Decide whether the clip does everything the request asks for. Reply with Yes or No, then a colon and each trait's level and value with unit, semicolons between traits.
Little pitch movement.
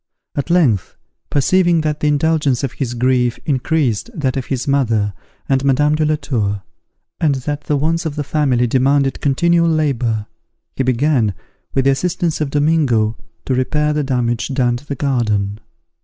No: average, 3.6 semitones